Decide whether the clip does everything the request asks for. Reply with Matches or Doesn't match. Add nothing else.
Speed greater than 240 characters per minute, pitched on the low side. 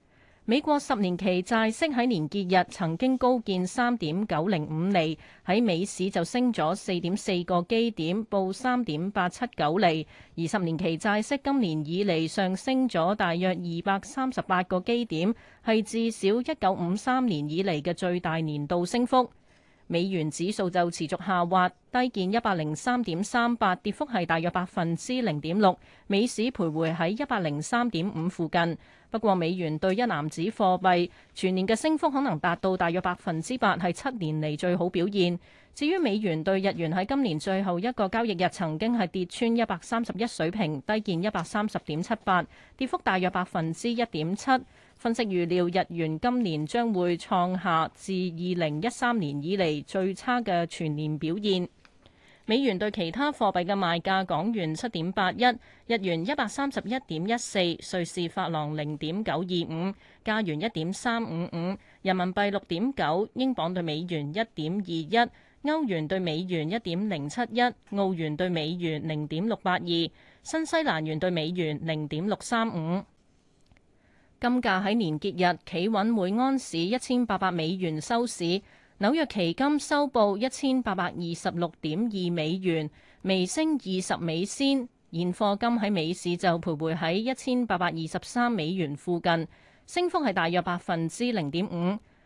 Doesn't match